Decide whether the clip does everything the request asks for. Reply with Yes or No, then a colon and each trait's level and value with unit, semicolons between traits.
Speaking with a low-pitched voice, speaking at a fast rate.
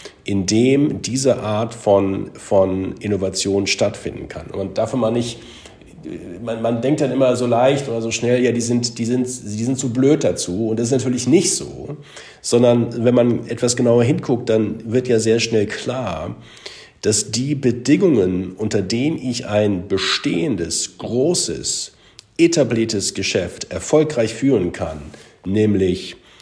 No: low, 115 Hz; average, 155 wpm